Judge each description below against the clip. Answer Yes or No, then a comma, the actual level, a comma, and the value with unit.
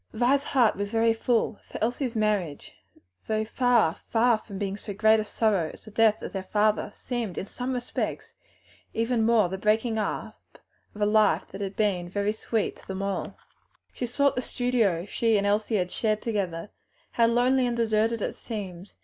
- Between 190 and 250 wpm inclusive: No, average, 175 wpm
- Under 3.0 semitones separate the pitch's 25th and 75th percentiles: Yes, narrow, 2.5 semitones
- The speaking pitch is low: No, high, 220 Hz